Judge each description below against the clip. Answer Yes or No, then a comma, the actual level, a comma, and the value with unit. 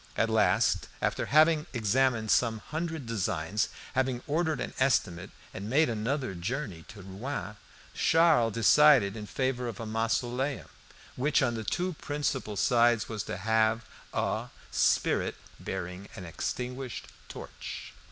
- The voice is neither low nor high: No, low, 120 Hz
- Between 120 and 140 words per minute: Yes, slow, 135 wpm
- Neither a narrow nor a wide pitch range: Yes, average, 4.3 semitones